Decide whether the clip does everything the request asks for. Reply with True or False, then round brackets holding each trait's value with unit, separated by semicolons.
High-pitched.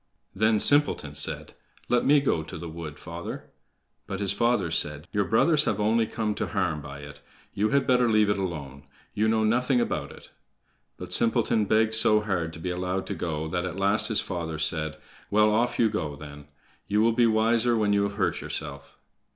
False (100 Hz)